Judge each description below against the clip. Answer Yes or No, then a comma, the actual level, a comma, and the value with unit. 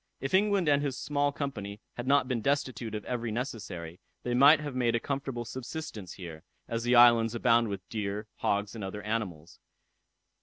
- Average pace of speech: Yes, average, 180 wpm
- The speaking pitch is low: Yes, low, 120 Hz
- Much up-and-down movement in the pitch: No, average, 4.6 semitones